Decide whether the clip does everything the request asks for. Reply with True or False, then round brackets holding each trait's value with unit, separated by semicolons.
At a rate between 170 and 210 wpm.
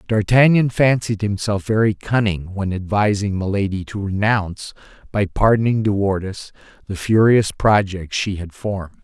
False (135 wpm)